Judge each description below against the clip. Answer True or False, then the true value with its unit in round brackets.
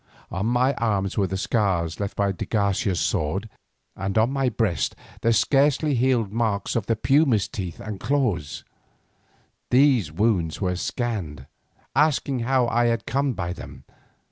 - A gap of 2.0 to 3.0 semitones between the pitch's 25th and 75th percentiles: False (4.6 semitones)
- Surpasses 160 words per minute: False (150 wpm)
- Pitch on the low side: True (110 Hz)